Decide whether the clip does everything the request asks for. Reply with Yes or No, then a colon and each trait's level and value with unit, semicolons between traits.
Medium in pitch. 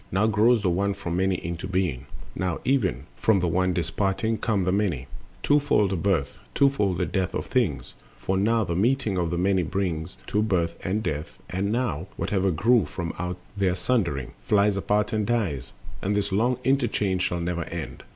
No: very low, 95 Hz